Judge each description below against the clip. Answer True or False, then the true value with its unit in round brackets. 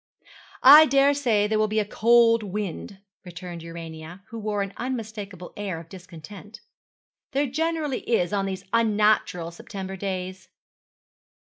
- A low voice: False (205 Hz)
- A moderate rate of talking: False (130 wpm)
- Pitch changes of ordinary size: True (3.9 semitones)